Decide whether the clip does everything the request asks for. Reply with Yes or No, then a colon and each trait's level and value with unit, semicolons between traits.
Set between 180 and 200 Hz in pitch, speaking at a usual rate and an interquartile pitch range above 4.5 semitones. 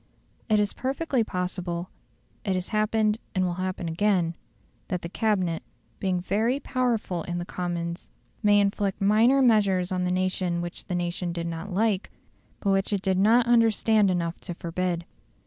No: high, 190 Hz; average, 165 wpm; average, 3.3 semitones